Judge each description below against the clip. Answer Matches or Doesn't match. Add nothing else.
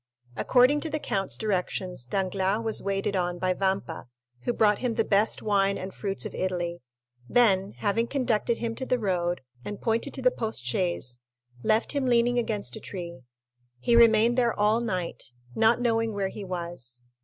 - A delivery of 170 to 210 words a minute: Matches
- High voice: Matches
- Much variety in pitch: Doesn't match